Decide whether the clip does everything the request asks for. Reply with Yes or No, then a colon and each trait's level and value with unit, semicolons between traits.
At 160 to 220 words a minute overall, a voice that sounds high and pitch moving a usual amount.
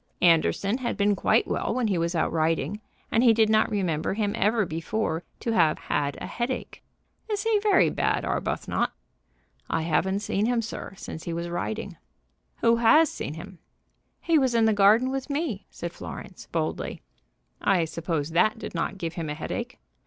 No: average, 180 wpm; high, 200 Hz; wide, 5.7 semitones